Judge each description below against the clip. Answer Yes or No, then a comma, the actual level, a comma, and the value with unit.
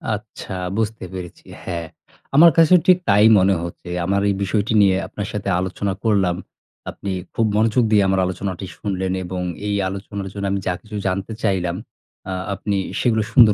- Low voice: Yes, low, 100 Hz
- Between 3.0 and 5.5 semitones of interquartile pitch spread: No, narrow, 2.4 semitones